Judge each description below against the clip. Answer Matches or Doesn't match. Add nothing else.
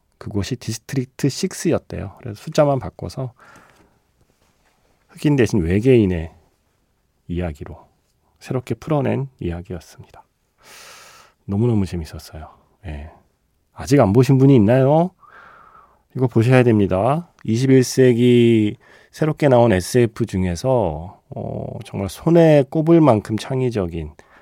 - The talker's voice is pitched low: Matches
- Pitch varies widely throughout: Matches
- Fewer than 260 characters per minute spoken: Matches